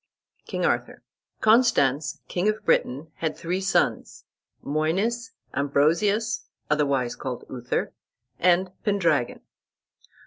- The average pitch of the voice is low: No, medium, 165 Hz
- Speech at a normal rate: No, slow, 95 wpm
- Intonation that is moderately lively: No, wide, 6.6 semitones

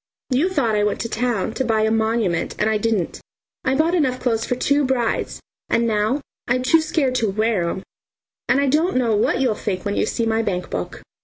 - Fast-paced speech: Yes, fast, 215 wpm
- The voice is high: Yes, high, 230 Hz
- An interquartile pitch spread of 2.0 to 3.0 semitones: No, average, 3.5 semitones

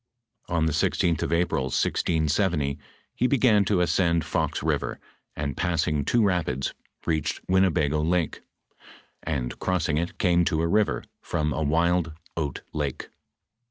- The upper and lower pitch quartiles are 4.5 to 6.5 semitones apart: No, average, 2.9 semitones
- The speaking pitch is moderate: No, very low, 85 Hz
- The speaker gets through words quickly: No, average, 140 wpm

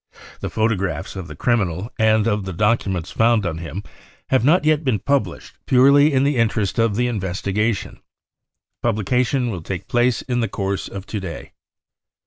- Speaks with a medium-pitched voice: No, low, 110 Hz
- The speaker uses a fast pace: No, average, 165 wpm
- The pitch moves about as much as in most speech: Yes, average, 4.3 semitones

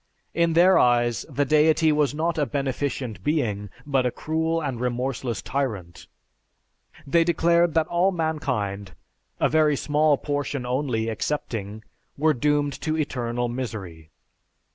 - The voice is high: No, medium, 140 Hz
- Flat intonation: No, average, 4.7 semitones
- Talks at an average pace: No, slow, 130 wpm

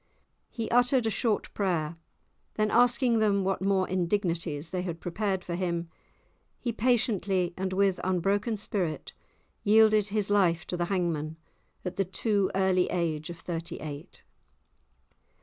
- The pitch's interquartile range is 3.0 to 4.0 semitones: Yes, average, 3.5 semitones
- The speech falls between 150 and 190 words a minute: No, average, 140 wpm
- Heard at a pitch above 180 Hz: Yes, high, 190 Hz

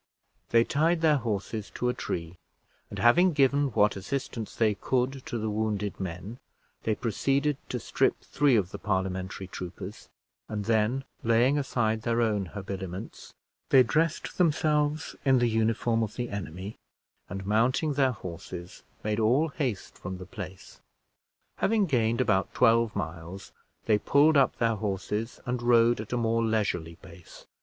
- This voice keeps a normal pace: Yes, average, 150 wpm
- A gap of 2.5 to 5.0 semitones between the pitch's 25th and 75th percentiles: Yes, average, 4.6 semitones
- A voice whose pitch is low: Yes, low, 115 Hz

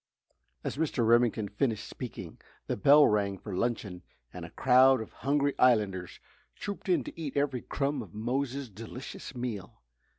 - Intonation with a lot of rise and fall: No, average, 4.7 semitones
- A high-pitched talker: No, low, 120 Hz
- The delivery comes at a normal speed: Yes, average, 155 wpm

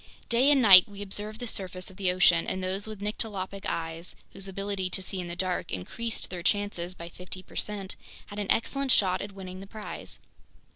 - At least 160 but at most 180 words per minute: No, average, 200 wpm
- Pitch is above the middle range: Yes, high, 195 Hz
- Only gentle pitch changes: Yes, narrow, 2.1 semitones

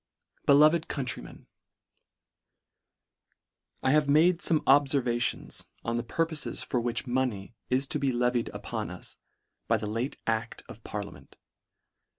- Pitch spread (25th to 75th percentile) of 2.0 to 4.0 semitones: Yes, average, 3.7 semitones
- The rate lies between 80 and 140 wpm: Yes, slow, 135 wpm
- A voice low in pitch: Yes, low, 125 Hz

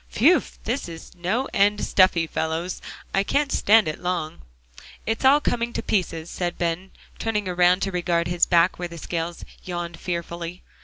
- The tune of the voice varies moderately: Yes, average, 3.3 semitones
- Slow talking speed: No, average, 165 wpm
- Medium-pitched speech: Yes, medium, 180 Hz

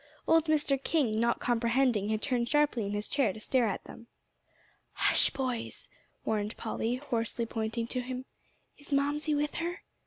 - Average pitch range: Yes, average, 4.1 semitones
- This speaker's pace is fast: No, average, 160 wpm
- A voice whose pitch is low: No, high, 245 Hz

